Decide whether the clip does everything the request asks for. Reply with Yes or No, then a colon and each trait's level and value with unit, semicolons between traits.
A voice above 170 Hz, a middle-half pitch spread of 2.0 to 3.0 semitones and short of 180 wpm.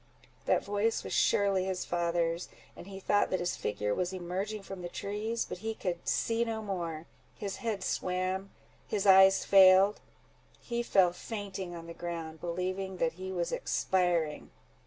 Yes: medium, 185 Hz; narrow, 2.5 semitones; average, 150 wpm